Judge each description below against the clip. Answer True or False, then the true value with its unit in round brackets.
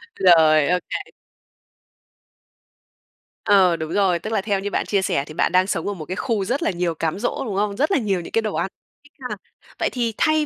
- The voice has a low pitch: False (195 Hz)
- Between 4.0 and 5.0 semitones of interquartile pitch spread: True (4.3 semitones)